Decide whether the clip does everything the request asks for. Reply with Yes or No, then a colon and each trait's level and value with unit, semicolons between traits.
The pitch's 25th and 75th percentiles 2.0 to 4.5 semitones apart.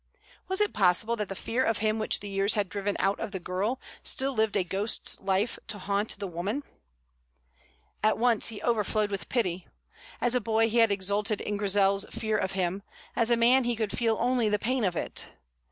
Yes: average, 2.8 semitones